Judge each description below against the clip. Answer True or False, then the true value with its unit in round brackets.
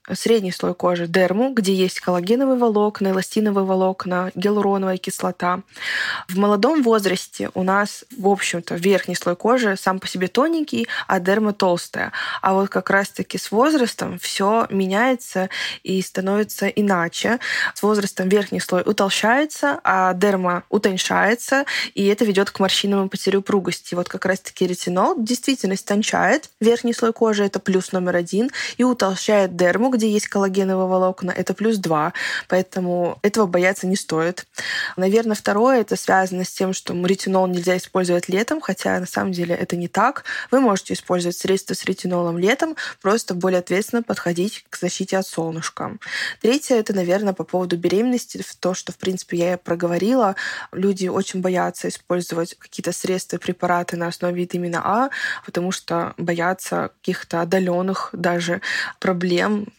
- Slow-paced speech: False (150 wpm)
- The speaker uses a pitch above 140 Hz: True (190 Hz)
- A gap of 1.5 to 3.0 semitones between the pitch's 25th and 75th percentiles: True (2.6 semitones)